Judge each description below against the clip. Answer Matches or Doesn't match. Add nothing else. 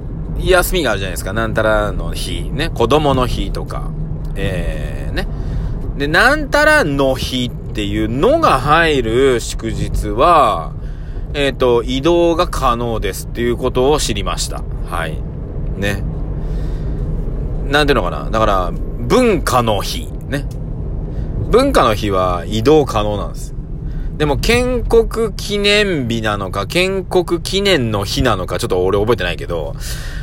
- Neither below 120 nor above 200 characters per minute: Doesn't match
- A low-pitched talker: Matches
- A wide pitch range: Matches